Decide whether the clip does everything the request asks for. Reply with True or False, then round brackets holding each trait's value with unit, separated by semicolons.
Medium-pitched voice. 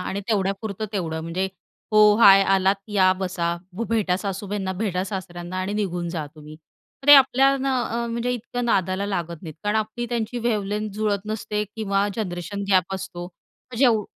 False (200 Hz)